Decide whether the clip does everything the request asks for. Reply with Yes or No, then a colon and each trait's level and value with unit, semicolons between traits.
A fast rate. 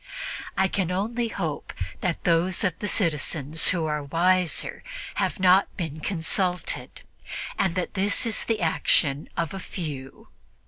No: average, 140 wpm